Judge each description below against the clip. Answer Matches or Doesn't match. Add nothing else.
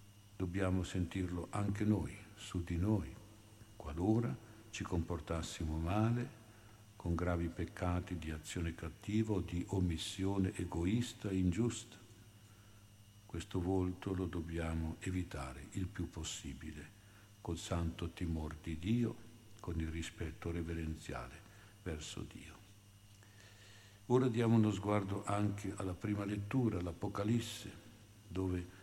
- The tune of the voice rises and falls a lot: Doesn't match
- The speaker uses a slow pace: Matches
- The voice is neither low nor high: Doesn't match